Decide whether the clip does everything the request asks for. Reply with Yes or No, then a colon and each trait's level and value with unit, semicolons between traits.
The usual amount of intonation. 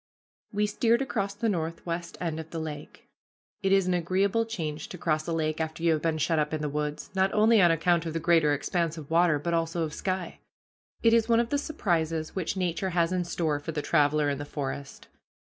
Yes: average, 3.4 semitones